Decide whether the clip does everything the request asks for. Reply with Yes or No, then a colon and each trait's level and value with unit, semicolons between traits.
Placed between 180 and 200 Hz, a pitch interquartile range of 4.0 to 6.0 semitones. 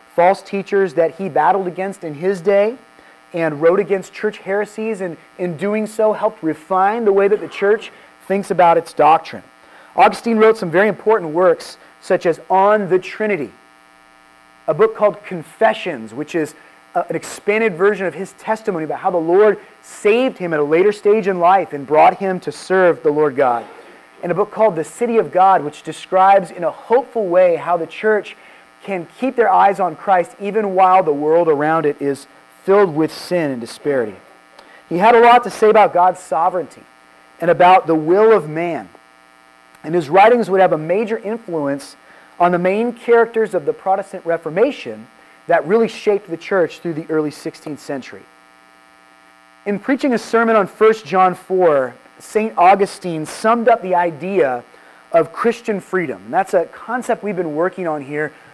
Yes: medium, 185 Hz; average, 5.1 semitones